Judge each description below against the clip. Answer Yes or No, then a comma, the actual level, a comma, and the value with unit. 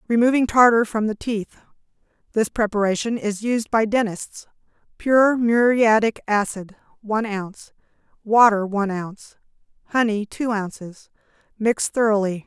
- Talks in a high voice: Yes, high, 215 Hz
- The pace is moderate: No, slow, 110 wpm